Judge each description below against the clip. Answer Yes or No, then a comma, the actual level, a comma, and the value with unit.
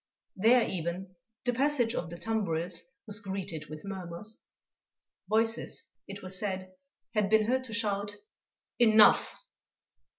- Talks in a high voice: Yes, high, 205 Hz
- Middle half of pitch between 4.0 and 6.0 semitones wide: No, average, 3.3 semitones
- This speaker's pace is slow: Yes, slow, 125 wpm